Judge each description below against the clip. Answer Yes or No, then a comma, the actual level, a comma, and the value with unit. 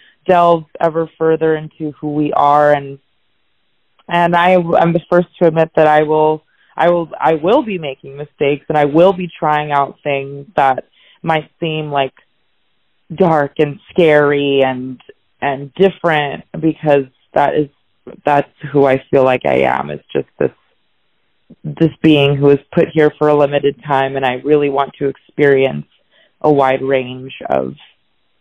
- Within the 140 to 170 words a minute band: Yes, average, 160 wpm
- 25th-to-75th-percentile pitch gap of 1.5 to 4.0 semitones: Yes, narrow, 2.6 semitones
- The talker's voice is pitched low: No, medium, 150 Hz